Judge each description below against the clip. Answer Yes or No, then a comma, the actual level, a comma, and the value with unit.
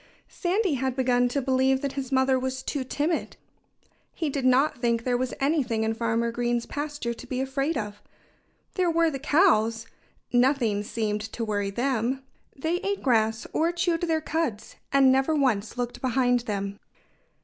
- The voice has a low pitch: No, very high, 260 Hz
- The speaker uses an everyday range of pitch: Yes, average, 3.8 semitones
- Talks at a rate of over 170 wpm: No, average, 165 wpm